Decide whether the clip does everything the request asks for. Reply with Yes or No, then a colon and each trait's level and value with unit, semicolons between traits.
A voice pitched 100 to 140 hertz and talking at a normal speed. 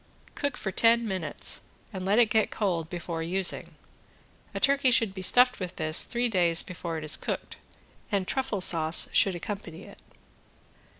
No: high, 190 Hz; average, 165 wpm